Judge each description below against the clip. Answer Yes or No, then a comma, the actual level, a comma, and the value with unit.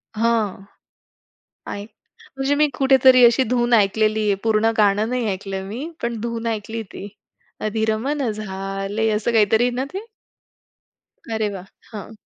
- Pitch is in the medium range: No, high, 220 Hz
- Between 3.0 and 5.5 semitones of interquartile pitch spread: No, narrow, 2.5 semitones